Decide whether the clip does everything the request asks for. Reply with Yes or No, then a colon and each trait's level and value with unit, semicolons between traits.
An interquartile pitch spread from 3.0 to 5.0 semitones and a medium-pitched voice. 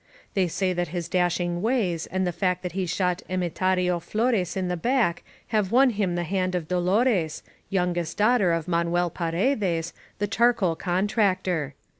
No: narrow, 2.5 semitones; medium, 180 Hz